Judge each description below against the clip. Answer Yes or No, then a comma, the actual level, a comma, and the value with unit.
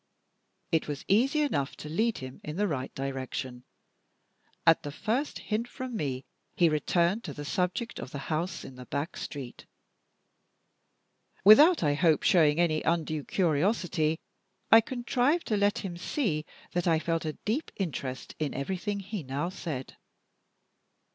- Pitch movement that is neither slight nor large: No, wide, 6.0 semitones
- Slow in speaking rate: No, average, 150 wpm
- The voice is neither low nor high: Yes, medium, 170 Hz